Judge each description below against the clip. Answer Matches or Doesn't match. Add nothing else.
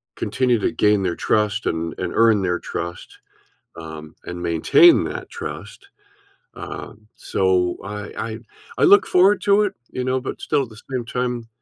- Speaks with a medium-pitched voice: Doesn't match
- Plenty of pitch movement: Matches